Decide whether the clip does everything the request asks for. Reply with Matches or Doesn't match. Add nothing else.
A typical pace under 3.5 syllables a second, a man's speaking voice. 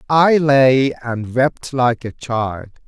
Matches